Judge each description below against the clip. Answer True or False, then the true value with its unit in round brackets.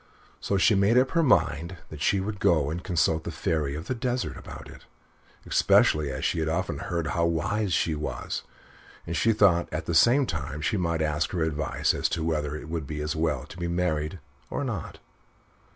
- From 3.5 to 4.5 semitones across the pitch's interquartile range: True (3.9 semitones)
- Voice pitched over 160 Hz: False (85 Hz)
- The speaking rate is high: True (210 wpm)